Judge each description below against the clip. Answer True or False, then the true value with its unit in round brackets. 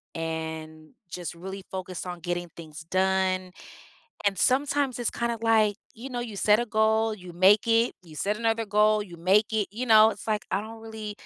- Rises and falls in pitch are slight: False (3.7 semitones)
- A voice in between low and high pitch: False (210 Hz)